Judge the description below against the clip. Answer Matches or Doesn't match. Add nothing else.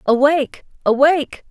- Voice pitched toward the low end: Doesn't match